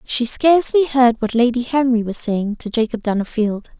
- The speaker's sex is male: No, female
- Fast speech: No, average, 175 wpm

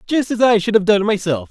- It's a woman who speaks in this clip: No, male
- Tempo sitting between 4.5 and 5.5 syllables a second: No, 5.8 syllables/s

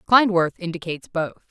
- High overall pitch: No, medium, 180 Hz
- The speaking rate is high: No, slow, 120 wpm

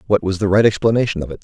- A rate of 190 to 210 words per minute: No, fast, 295 wpm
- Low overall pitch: Yes, low, 100 Hz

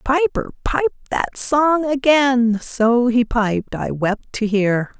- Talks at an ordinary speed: Yes, average, 145 wpm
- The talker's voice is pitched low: No, very high, 250 Hz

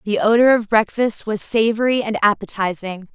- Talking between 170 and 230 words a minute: No, average, 155 wpm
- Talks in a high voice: Yes, high, 215 Hz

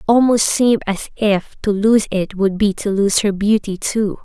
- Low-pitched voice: No, high, 205 Hz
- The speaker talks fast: Yes, fast, 210 wpm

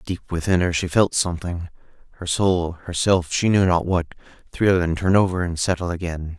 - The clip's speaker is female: No, male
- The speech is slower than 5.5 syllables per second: Yes, 5.1 syllables/s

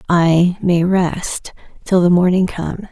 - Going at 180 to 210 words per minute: No, average, 145 wpm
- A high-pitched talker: No, medium, 175 Hz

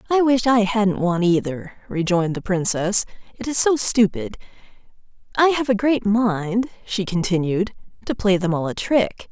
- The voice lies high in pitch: Yes, high, 205 Hz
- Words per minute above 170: No, average, 165 wpm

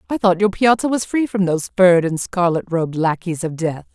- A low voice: No, medium, 185 Hz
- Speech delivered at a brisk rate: Yes, fast, 230 wpm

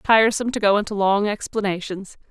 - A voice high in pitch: Yes, high, 205 Hz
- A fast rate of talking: No, average, 155 wpm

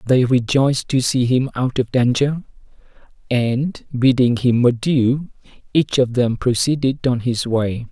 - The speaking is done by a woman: No, male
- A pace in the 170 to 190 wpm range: No, average, 145 wpm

